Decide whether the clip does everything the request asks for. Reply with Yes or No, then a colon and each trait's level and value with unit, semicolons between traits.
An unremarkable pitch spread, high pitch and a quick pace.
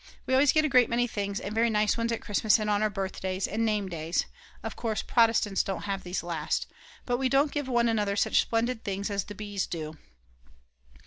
Yes: average, 3.1 semitones; high, 210 Hz; fast, 215 wpm